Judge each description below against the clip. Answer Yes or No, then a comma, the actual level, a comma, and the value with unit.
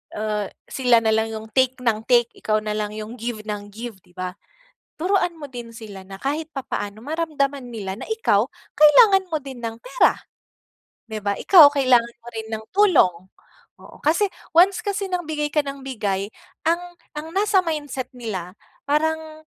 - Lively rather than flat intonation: Yes, wide, 6.7 semitones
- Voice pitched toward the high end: Yes, very high, 255 Hz